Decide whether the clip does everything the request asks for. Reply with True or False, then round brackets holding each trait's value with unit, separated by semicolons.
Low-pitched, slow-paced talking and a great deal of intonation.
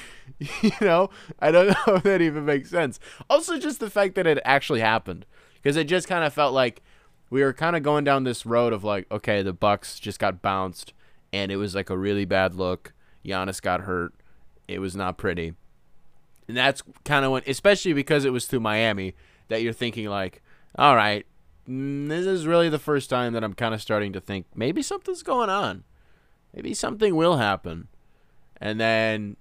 False (115 Hz; 195 wpm; 7.6 semitones)